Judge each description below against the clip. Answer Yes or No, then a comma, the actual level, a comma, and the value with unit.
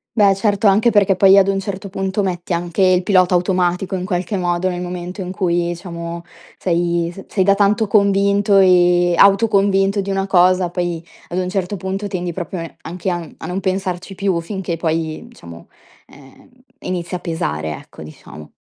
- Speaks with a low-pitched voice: No, medium, 185 Hz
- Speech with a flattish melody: Yes, narrow, 2.0 semitones